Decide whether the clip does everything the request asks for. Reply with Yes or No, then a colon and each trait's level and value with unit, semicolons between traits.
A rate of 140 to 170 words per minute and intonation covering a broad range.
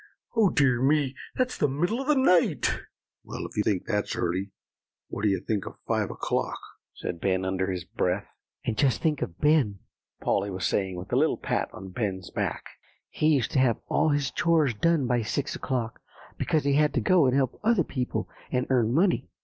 No: average, 200 wpm; wide, 7.2 semitones